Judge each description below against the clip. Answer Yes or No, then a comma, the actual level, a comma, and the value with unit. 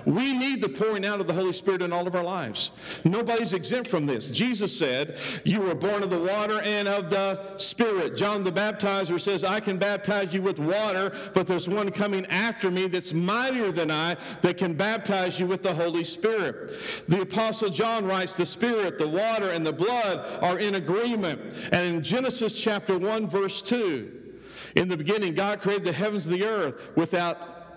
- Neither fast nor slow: Yes, average, 195 wpm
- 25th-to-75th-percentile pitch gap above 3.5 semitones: No, average, 2.9 semitones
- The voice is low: No, high, 195 Hz